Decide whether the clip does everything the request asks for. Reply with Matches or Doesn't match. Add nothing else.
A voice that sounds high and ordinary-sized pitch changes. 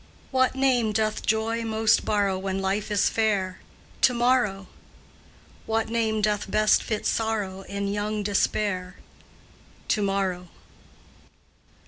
Doesn't match